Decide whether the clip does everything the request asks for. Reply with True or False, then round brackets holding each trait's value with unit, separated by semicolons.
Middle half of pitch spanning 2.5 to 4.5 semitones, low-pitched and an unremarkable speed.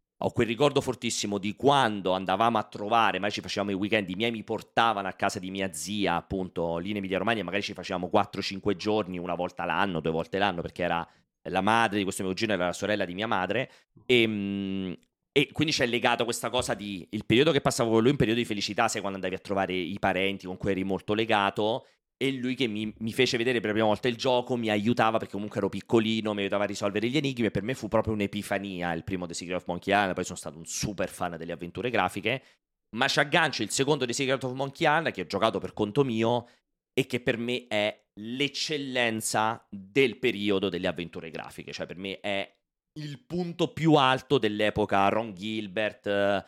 False (3.5 semitones; 105 Hz; 215 wpm)